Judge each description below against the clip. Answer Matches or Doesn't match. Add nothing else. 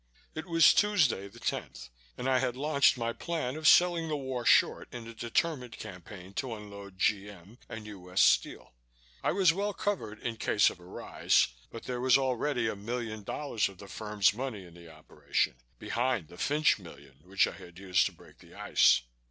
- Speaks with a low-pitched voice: Matches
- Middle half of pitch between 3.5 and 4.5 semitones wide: Doesn't match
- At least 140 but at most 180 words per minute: Doesn't match